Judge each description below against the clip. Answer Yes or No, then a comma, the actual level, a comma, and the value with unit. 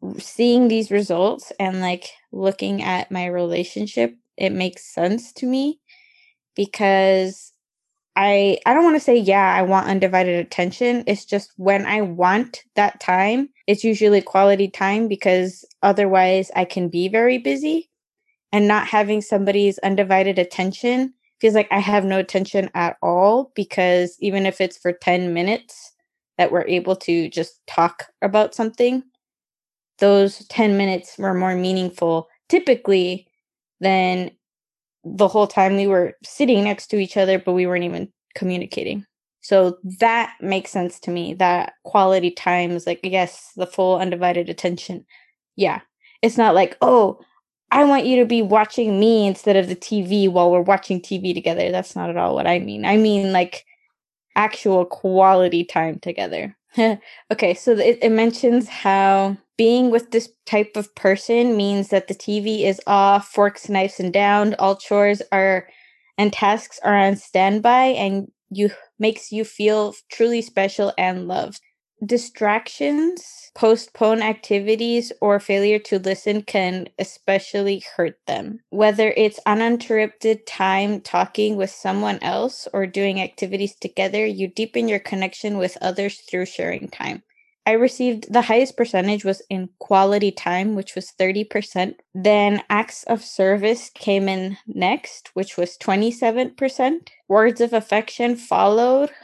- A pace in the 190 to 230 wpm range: No, average, 150 wpm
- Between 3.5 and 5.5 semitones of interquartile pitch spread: No, average, 2.9 semitones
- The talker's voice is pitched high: Yes, high, 200 Hz